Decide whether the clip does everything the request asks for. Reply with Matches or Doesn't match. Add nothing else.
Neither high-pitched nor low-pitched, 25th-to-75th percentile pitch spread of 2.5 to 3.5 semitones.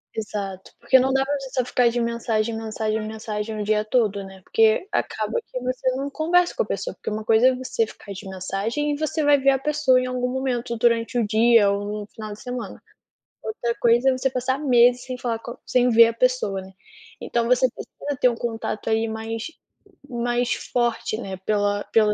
Doesn't match